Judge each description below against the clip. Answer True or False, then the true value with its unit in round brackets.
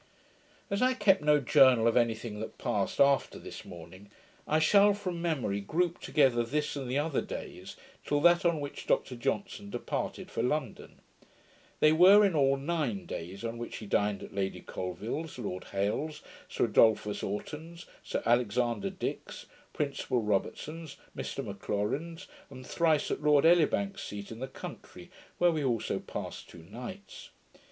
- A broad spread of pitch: True (6.8 semitones)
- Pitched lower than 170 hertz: True (135 Hz)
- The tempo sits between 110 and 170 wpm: True (160 wpm)